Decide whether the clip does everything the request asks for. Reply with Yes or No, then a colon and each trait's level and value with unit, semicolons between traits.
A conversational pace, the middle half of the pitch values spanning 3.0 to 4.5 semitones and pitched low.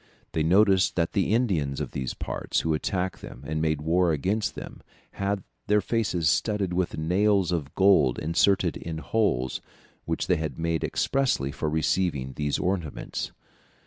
Yes: average, 155 wpm; average, 4.1 semitones; very low, 85 Hz